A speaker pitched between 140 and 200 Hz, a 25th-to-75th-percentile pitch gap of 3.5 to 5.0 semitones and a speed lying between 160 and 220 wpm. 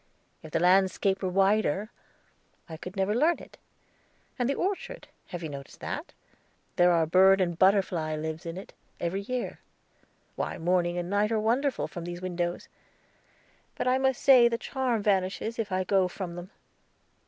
Yes: high, 190 Hz; average, 4.1 semitones; average, 165 wpm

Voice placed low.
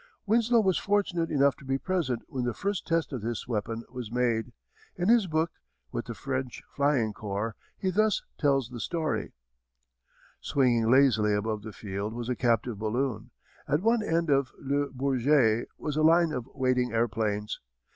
Yes: low, 130 Hz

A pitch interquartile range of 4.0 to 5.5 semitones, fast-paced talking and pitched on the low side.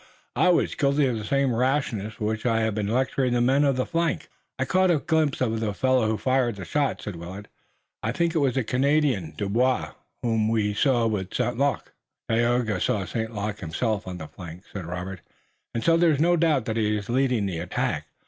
Yes: average, 4.7 semitones; fast, 215 wpm; low, 115 Hz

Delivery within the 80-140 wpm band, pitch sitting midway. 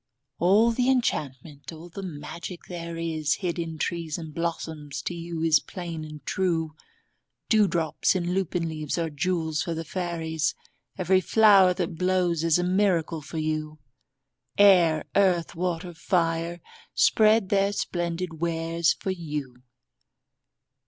Yes: slow, 135 wpm; medium, 170 Hz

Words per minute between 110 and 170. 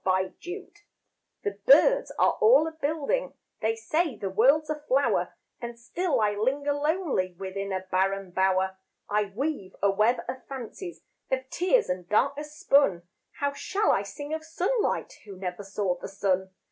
Yes: average, 160 wpm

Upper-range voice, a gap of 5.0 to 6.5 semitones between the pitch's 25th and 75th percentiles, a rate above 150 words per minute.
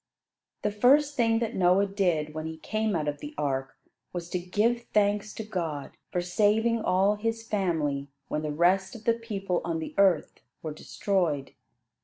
Yes: high, 195 Hz; average, 5.3 semitones; average, 175 wpm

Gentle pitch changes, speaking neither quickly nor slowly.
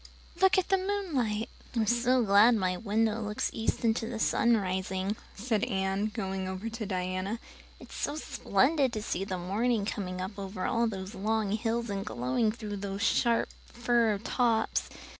No: average, 3.3 semitones; average, 160 wpm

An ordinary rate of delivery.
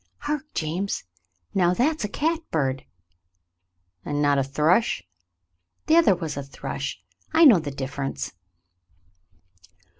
No: slow, 120 wpm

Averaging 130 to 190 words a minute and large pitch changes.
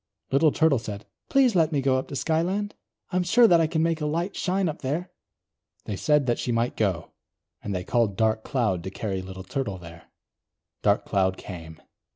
No: average, 200 wpm; wide, 8.6 semitones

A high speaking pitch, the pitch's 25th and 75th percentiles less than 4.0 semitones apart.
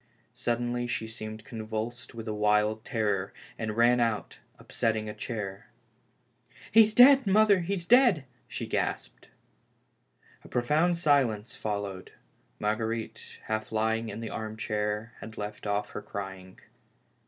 No: low, 110 Hz; narrow, 2.6 semitones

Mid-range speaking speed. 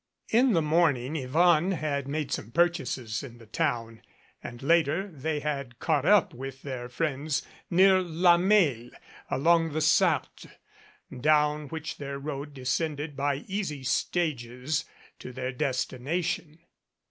No: slow, 130 wpm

